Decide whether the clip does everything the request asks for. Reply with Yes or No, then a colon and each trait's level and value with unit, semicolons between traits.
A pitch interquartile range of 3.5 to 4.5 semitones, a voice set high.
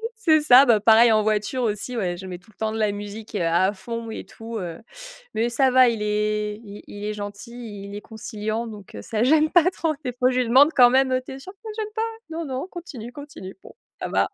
Yes: average, 3.8 semitones; high, 225 Hz